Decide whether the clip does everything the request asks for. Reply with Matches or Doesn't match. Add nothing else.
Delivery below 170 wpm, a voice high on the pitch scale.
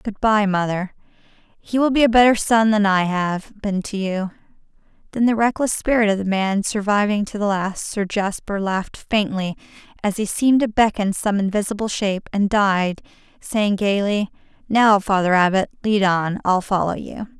Doesn't match